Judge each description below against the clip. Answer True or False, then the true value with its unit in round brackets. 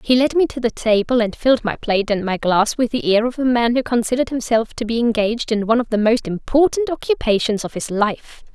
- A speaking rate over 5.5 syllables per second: True (6.0 syllables/s)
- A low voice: False (235 Hz)